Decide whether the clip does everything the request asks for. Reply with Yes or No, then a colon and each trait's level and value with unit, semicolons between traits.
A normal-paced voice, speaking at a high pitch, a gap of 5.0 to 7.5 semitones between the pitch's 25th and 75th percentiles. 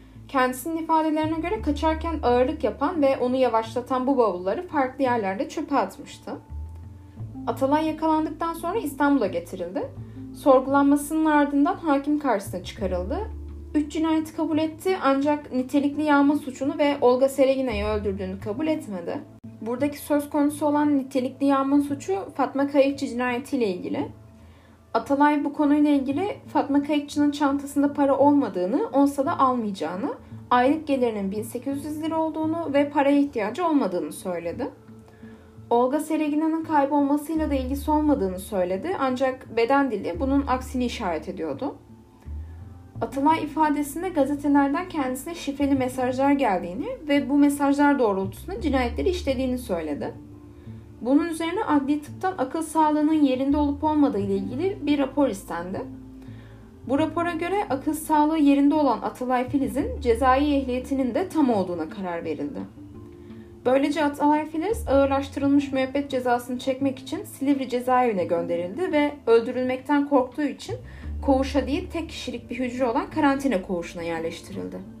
Yes: average, 125 wpm; very high, 275 Hz; wide, 5.5 semitones